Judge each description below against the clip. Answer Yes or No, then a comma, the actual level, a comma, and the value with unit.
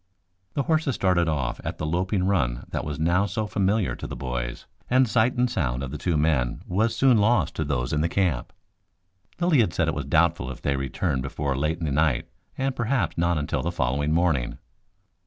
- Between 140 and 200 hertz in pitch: No, very low, 80 Hz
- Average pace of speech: No, fast, 210 wpm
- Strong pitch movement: Yes, wide, 6.6 semitones